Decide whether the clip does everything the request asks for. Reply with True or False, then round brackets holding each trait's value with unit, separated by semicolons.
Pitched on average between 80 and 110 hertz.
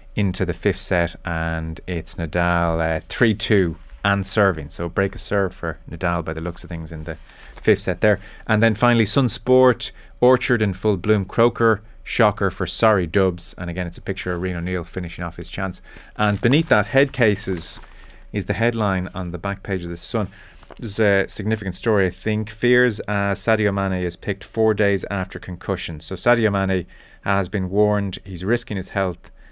True (95 Hz)